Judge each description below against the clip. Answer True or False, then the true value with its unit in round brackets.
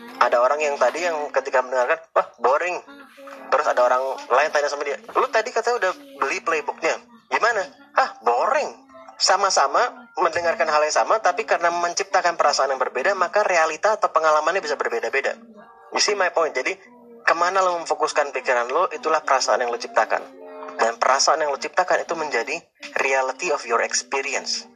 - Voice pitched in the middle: True (160 Hz)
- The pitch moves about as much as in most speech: False (5.9 semitones)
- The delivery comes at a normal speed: False (165 wpm)